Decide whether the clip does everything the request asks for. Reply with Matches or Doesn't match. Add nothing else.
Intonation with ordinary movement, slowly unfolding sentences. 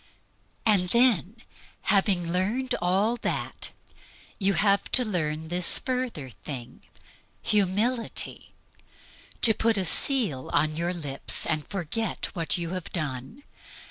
Doesn't match